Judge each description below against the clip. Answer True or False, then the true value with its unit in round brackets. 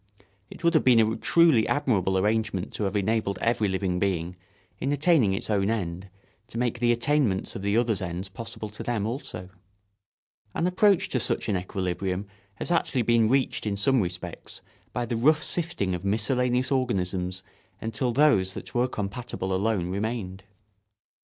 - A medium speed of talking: True (165 wpm)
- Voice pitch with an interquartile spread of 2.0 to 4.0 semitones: False (4.5 semitones)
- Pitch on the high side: False (110 Hz)